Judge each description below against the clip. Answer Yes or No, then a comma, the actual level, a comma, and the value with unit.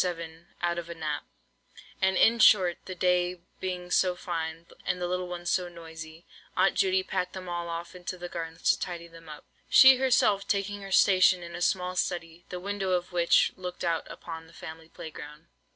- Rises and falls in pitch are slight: Yes, narrow, 1.8 semitones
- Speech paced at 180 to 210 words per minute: Yes, average, 200 wpm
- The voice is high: No, medium, 175 Hz